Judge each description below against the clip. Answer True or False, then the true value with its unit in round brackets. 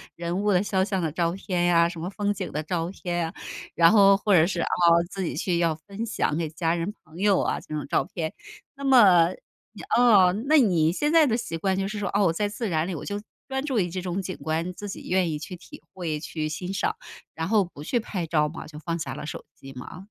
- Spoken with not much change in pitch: False (3.6 semitones)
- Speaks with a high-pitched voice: False (180 Hz)